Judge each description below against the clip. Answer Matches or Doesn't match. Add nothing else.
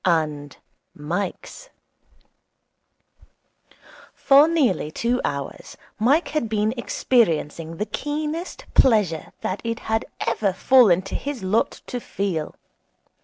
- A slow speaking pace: Matches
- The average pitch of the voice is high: Matches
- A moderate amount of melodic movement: Doesn't match